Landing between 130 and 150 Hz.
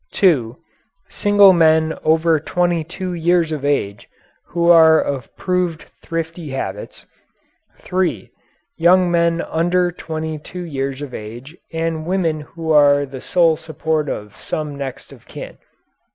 No: medium, 160 Hz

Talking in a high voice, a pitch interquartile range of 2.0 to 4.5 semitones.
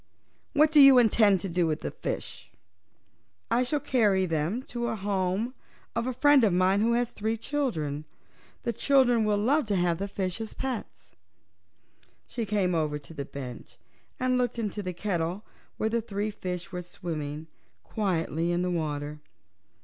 No: high, 200 Hz; wide, 5.4 semitones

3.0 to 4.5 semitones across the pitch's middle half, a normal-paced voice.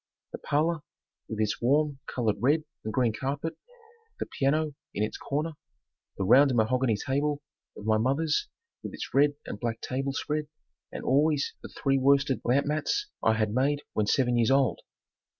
Yes: average, 4.1 semitones; average, 170 wpm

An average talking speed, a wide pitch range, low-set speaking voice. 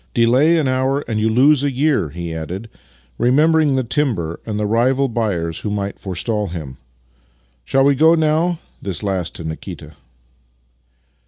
Yes: average, 165 wpm; wide, 7.8 semitones; low, 115 Hz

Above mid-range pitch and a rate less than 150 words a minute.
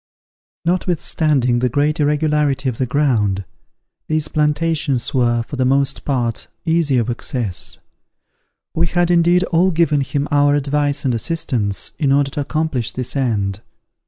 No: medium, 145 Hz; average, 140 wpm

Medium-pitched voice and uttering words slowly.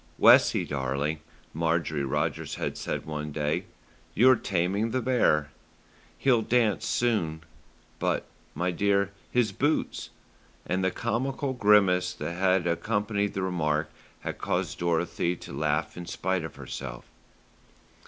No: very low, 90 Hz; slow, 125 wpm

